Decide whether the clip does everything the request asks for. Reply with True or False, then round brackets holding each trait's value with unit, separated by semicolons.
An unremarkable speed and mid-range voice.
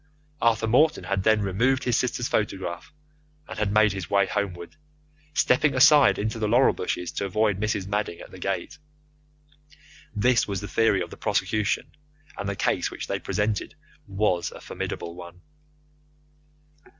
False (155 wpm; 105 Hz)